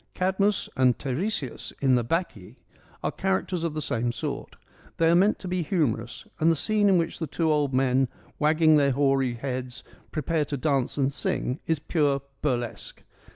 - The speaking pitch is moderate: Yes, medium, 150 Hz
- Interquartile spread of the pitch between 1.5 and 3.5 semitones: No, average, 4.5 semitones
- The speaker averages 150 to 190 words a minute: Yes, average, 175 wpm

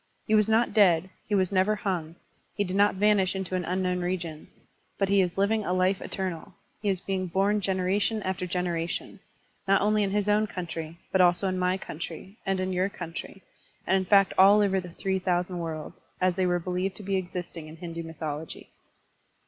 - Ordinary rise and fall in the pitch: No, narrow, 1.9 semitones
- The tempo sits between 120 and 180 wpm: No, average, 195 wpm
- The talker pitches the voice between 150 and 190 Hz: Yes, medium, 185 Hz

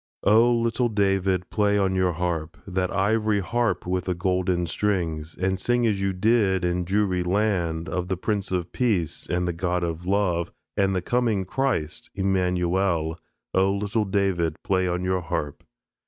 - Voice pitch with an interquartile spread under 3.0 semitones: Yes, narrow, 2.5 semitones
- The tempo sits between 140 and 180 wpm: Yes, average, 165 wpm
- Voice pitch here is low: Yes, very low, 95 Hz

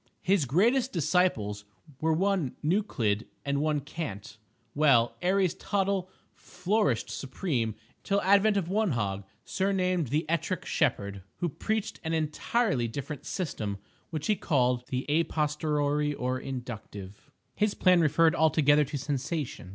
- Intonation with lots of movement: Yes, wide, 6.4 semitones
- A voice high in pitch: No, medium, 155 Hz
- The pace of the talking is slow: Yes, slow, 130 wpm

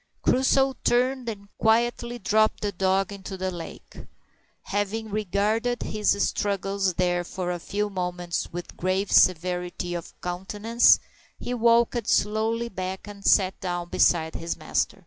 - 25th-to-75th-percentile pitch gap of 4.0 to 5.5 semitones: No, average, 3.5 semitones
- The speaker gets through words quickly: No, slow, 135 wpm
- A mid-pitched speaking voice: No, high, 200 Hz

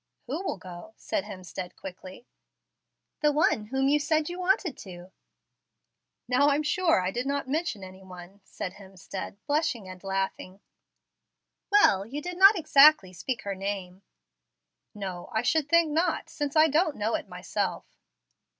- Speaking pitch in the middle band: No, high, 235 Hz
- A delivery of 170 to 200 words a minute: No, average, 150 wpm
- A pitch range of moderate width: No, wide, 8.3 semitones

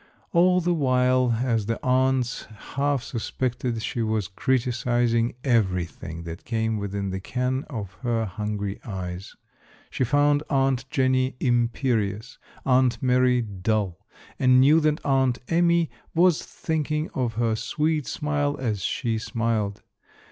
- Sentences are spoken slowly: Yes, slow, 125 wpm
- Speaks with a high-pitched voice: No, low, 125 Hz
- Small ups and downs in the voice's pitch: No, average, 3.6 semitones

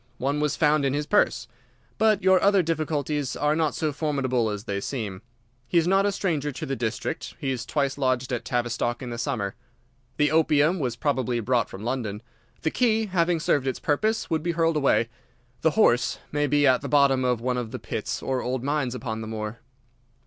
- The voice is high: No, medium, 140 Hz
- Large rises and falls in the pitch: No, average, 4.4 semitones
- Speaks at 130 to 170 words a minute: No, fast, 205 wpm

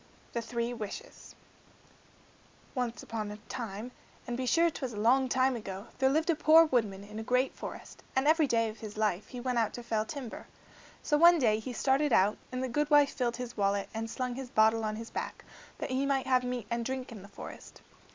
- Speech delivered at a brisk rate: Yes, fast, 220 wpm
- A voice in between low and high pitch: No, high, 245 Hz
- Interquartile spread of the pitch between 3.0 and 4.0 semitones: Yes, average, 3.3 semitones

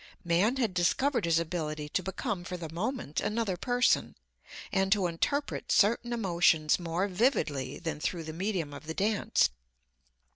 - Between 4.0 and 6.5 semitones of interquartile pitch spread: Yes, average, 4.9 semitones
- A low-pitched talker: No, medium, 180 Hz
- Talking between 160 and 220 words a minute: No, average, 150 wpm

